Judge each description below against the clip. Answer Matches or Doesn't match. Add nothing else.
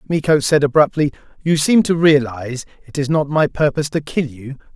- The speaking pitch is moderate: Matches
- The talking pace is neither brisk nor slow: Matches